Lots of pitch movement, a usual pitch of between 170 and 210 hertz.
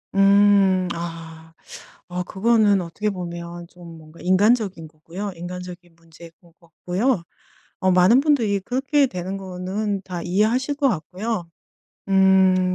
No: average, 3.1 semitones; medium, 185 Hz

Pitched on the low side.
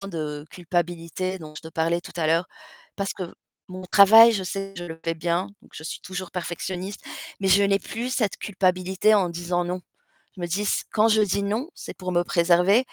No: medium, 185 Hz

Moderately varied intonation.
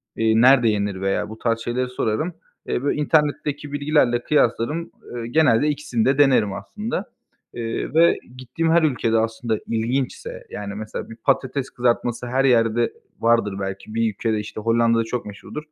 Yes: average, 3.9 semitones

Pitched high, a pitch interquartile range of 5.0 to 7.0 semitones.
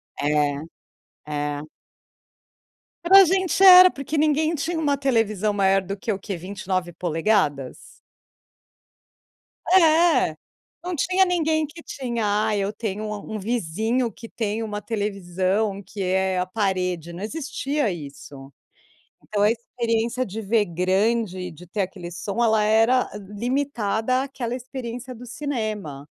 Yes: high, 215 Hz; average, 5.3 semitones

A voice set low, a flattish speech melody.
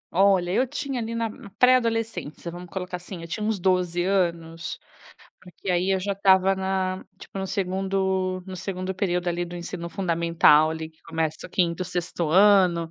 No: medium, 185 Hz; narrow, 2.1 semitones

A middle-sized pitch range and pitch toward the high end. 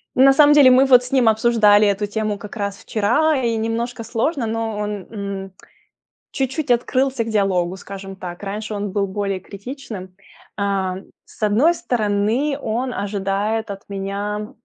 Yes: average, 3.4 semitones; high, 215 Hz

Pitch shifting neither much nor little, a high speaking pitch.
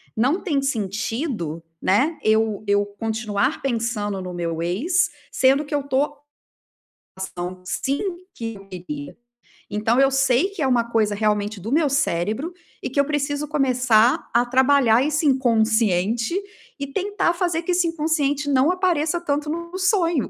No: wide, 5.7 semitones; very high, 260 Hz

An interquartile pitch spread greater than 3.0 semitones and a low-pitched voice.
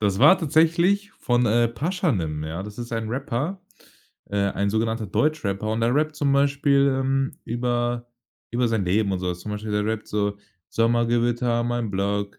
Yes: average, 4.9 semitones; low, 120 Hz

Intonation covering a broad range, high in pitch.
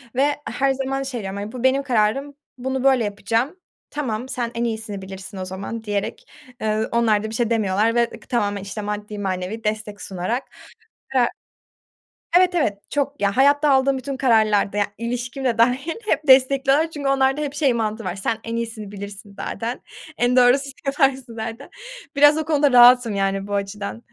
No: average, 4.5 semitones; high, 235 Hz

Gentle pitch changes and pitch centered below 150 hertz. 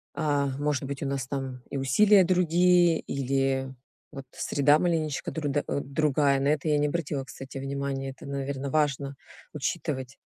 Yes: narrow, 2.2 semitones; medium, 140 Hz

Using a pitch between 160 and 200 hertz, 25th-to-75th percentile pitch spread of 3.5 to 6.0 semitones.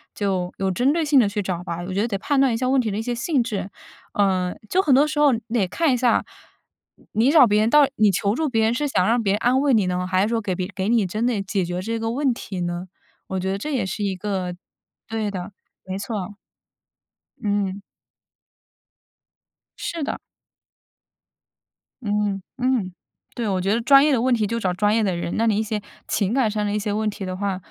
No: high, 210 Hz; average, 4.1 semitones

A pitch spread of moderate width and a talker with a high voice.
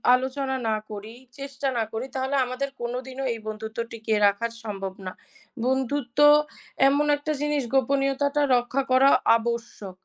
Yes: average, 3.4 semitones; very high, 255 Hz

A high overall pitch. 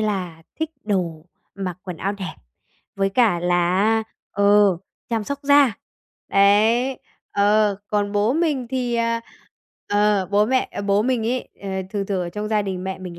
Yes: high, 205 Hz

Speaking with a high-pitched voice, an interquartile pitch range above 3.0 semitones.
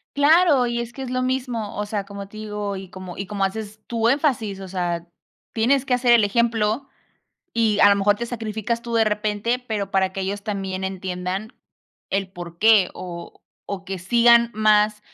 Yes: high, 210 Hz; average, 3.4 semitones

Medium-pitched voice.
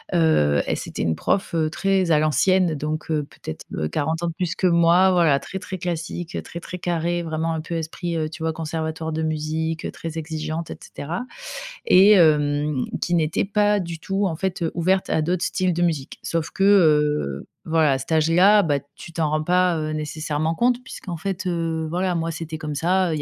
Yes: medium, 165 Hz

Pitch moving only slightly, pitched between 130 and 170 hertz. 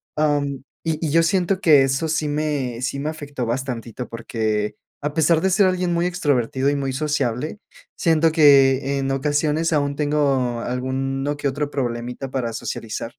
No: average, 3.0 semitones; medium, 140 Hz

